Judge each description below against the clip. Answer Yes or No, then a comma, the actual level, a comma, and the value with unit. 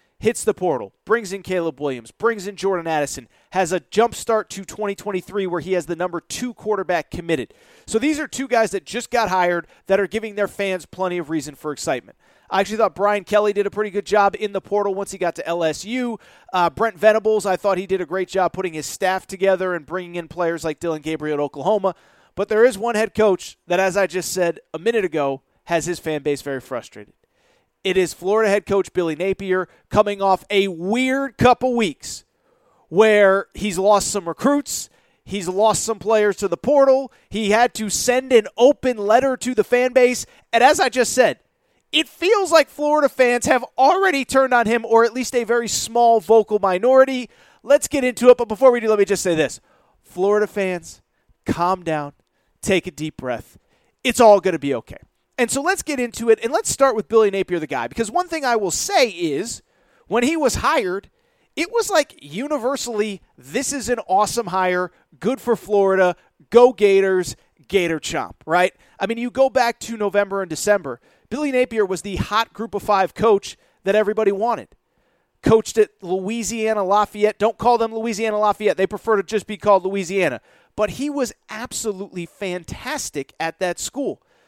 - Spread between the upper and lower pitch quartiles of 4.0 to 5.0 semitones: Yes, average, 4.3 semitones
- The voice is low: No, high, 205 Hz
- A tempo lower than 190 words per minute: No, average, 195 wpm